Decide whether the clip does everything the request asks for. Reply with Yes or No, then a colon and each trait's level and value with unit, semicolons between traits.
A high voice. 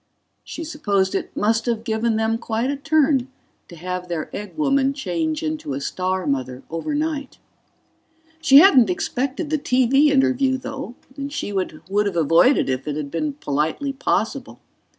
Yes: high, 230 Hz